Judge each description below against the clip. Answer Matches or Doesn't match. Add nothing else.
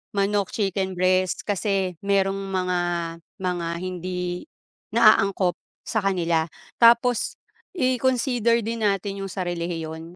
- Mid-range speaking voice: Doesn't match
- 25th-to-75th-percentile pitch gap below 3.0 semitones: Matches